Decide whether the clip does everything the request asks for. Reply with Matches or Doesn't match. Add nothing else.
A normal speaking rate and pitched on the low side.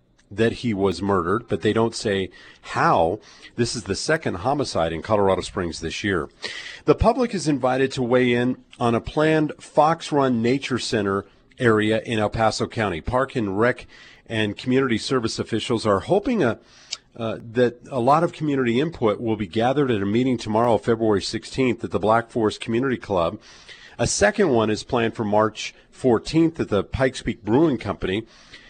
Matches